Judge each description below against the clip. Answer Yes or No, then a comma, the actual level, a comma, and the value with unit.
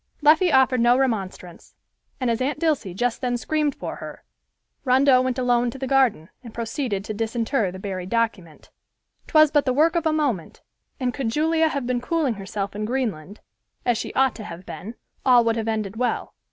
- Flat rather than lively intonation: No, average, 3.9 semitones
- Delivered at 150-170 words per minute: No, average, 190 wpm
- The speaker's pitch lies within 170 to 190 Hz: No, high, 245 Hz